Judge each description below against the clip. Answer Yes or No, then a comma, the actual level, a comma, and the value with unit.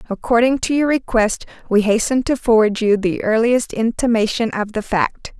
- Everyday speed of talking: Yes, average, 165 wpm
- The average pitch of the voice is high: Yes, high, 230 Hz